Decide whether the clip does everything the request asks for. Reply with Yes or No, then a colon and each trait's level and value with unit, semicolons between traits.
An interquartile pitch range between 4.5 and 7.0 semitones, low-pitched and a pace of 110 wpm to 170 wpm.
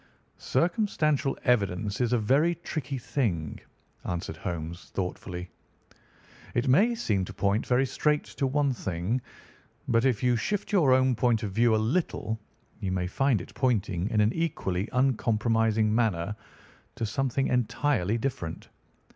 Yes: average, 5.3 semitones; low, 115 Hz; average, 140 wpm